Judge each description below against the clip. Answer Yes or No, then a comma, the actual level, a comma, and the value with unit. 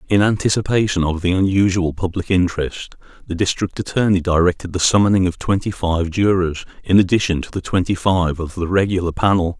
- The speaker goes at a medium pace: Yes, average, 170 wpm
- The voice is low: Yes, very low, 90 Hz